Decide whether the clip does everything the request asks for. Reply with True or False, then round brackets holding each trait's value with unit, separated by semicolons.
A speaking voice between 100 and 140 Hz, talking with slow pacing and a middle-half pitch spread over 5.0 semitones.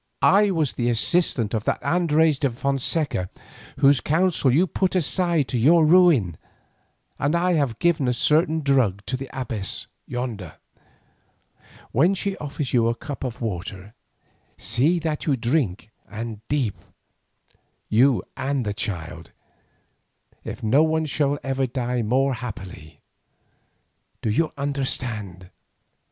True (135 Hz; 130 wpm; 5.5 semitones)